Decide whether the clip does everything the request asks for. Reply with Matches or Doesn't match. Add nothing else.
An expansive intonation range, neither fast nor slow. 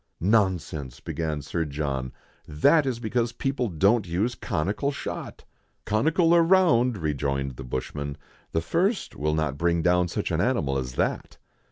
Matches